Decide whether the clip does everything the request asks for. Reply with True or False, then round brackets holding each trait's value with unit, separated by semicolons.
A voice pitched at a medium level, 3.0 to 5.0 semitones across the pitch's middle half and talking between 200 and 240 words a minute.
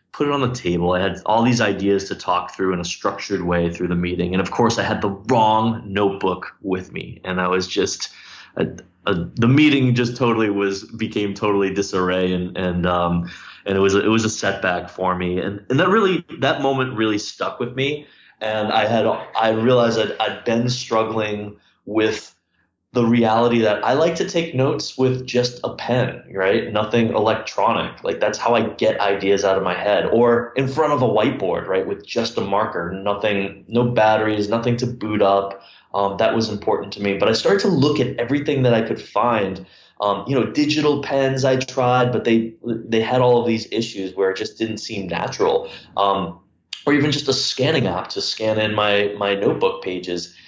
False (110 Hz; 3.8 semitones; 205 wpm)